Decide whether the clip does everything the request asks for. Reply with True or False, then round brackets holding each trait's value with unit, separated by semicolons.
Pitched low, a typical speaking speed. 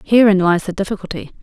False (190 Hz; 170 wpm)